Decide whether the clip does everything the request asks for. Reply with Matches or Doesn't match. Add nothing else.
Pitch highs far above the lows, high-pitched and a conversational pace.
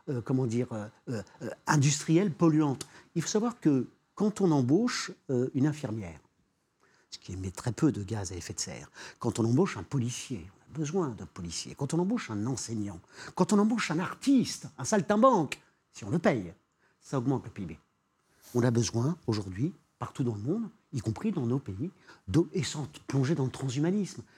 Doesn't match